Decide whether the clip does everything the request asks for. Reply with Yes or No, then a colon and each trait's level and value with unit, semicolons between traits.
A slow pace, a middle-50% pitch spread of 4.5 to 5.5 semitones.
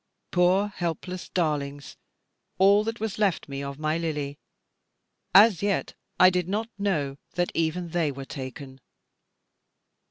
Yes: slow, 130 wpm; average, 5.2 semitones